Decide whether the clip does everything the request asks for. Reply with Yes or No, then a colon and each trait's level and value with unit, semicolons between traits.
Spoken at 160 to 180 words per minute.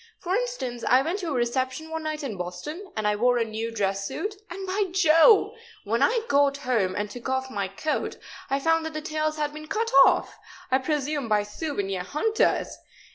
No: average, 200 wpm